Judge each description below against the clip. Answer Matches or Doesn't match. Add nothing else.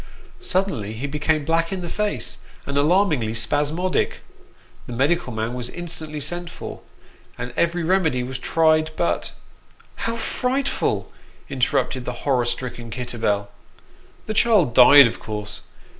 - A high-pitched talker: Doesn't match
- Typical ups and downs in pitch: Doesn't match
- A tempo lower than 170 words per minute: Matches